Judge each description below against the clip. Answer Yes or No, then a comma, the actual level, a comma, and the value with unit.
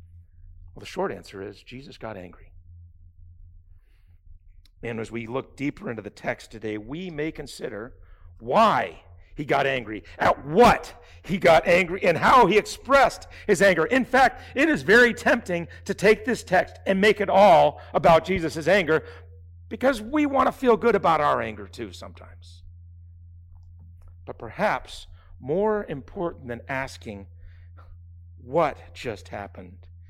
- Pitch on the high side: No, low, 105 Hz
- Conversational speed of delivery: Yes, average, 145 wpm